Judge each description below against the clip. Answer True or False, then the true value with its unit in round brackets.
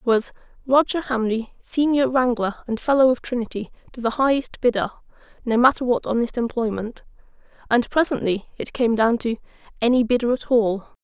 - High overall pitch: True (240 Hz)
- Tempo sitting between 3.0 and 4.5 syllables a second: False (5.3 syllables/s)